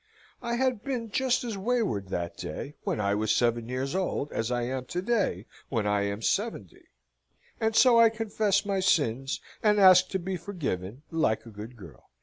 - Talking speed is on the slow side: No, average, 185 wpm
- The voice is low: No, medium, 165 Hz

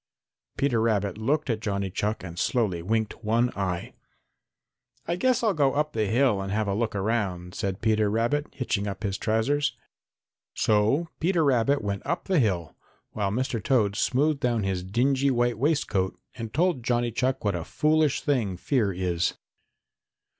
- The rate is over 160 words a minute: Yes, average, 170 wpm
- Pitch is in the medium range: No, low, 115 Hz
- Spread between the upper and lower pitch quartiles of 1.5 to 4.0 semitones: No, wide, 5.5 semitones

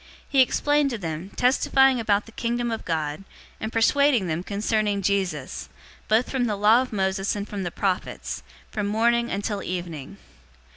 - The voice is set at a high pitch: Yes, high, 210 Hz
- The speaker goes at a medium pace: Yes, average, 160 wpm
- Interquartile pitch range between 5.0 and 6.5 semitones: No, average, 3.8 semitones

